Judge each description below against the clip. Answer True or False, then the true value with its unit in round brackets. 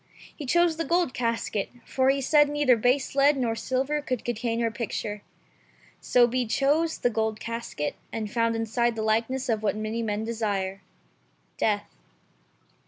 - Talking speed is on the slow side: False (165 wpm)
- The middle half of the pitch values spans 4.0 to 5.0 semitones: False (3.5 semitones)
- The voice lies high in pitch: True (235 Hz)